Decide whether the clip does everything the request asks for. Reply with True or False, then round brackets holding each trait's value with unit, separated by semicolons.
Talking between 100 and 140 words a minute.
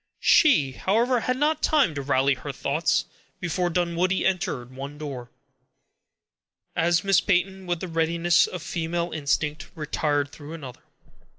True (135 wpm)